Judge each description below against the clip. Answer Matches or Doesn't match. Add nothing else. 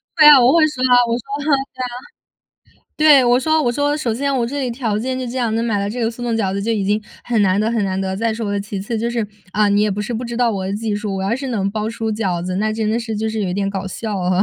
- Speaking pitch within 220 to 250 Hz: Matches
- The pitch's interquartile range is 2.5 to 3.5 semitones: Matches